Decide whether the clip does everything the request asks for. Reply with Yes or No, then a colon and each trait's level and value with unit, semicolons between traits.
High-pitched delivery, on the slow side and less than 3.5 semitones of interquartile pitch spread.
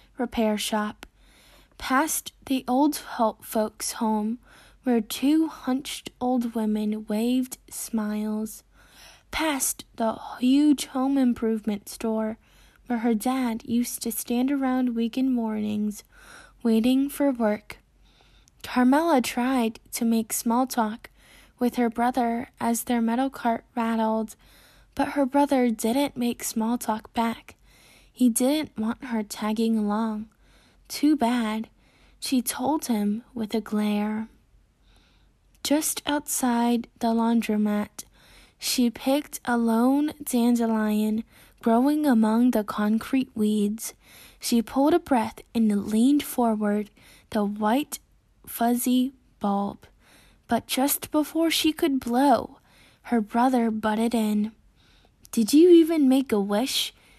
Yes: high, 235 Hz; slow, 115 wpm; average, 3.1 semitones